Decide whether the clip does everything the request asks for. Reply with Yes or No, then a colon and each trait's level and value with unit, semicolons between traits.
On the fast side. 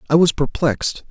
No: average, 165 wpm